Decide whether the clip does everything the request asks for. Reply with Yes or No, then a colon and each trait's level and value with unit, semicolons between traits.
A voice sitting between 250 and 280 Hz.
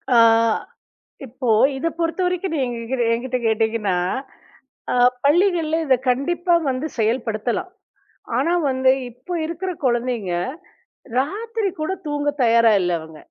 Yes: very high, 260 Hz